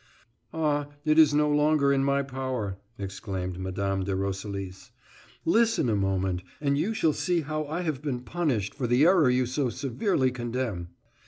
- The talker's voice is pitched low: Yes, low, 130 Hz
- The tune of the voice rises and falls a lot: Yes, wide, 7.2 semitones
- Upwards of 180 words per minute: No, average, 165 wpm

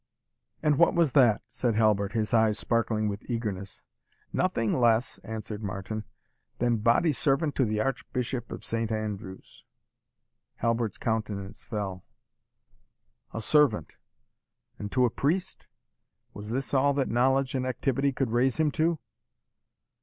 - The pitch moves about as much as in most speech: Yes, average, 3.8 semitones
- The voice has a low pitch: Yes, low, 115 Hz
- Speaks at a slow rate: Yes, slow, 130 wpm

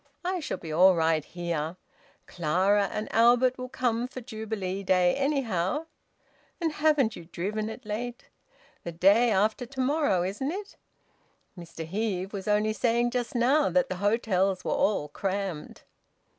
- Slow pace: No, average, 150 wpm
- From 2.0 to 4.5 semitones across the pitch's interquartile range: No, average, 5.3 semitones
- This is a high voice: Yes, high, 215 Hz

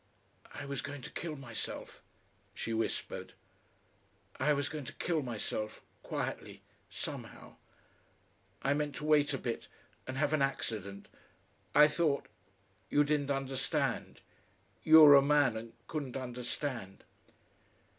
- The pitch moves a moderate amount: Yes, average, 3.1 semitones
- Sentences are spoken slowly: Yes, slow, 125 wpm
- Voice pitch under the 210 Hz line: Yes, medium, 140 Hz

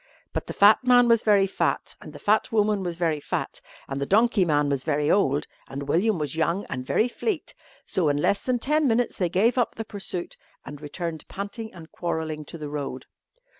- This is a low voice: No, medium, 180 Hz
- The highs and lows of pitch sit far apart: Yes, wide, 6.5 semitones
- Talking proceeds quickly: Yes, fast, 210 wpm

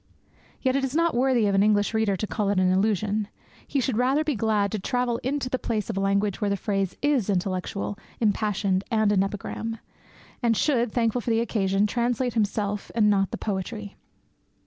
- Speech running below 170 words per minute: No, average, 195 wpm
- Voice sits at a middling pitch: No, high, 215 Hz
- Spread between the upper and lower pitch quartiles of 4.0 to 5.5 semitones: No, average, 3.3 semitones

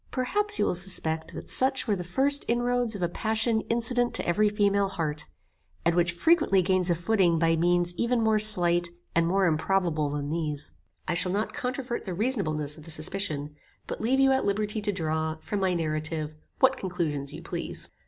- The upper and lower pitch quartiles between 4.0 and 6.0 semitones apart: Yes, average, 5.2 semitones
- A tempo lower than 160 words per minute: No, average, 190 wpm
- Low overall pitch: No, medium, 185 Hz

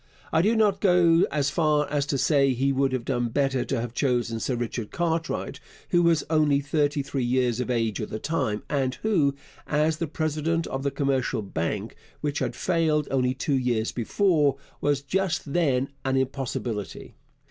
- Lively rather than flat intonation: No, average, 3.8 semitones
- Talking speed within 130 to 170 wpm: No, average, 180 wpm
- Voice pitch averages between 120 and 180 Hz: Yes, medium, 140 Hz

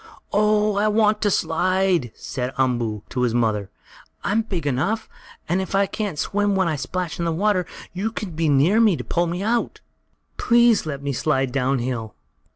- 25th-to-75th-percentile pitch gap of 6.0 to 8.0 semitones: Yes, wide, 7.5 semitones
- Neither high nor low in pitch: Yes, medium, 175 Hz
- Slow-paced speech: No, average, 180 wpm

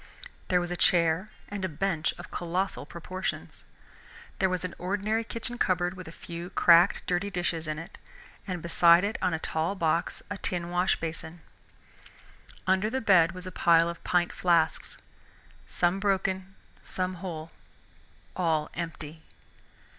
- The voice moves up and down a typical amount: No, narrow, 2.1 semitones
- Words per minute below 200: Yes, average, 145 wpm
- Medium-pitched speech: Yes, medium, 180 Hz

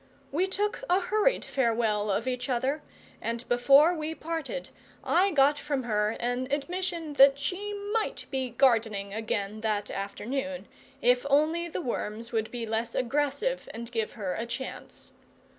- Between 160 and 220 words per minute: No, average, 150 wpm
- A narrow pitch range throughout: No, average, 5.3 semitones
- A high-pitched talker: Yes, very high, 260 Hz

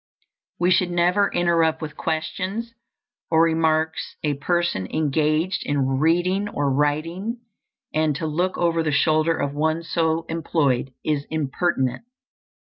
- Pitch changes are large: No, narrow, 2.6 semitones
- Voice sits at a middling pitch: Yes, medium, 160 Hz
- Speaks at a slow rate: Yes, slow, 130 wpm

